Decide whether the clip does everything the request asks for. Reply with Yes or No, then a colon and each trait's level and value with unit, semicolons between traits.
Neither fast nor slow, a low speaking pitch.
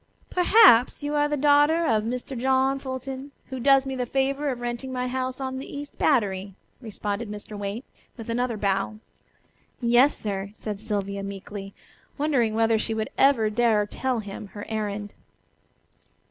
No: average, 160 wpm; high, 240 Hz